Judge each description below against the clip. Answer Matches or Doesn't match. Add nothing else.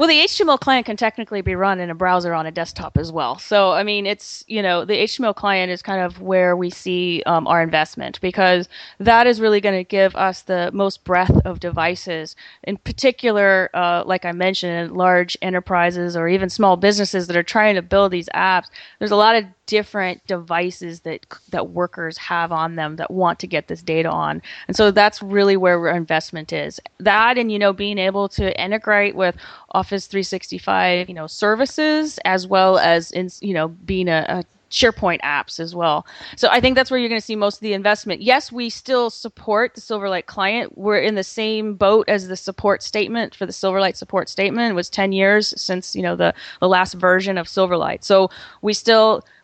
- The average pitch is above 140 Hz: Matches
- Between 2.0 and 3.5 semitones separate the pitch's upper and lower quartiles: Matches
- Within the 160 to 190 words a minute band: Doesn't match